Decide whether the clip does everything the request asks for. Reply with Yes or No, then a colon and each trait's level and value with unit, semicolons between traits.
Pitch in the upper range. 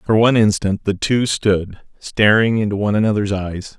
No: low, 105 Hz